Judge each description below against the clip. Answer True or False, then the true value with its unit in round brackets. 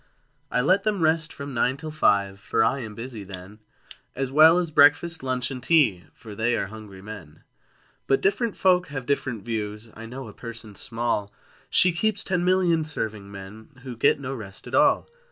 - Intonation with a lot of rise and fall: True (6.6 semitones)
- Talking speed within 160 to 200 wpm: True (190 wpm)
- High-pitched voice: False (125 Hz)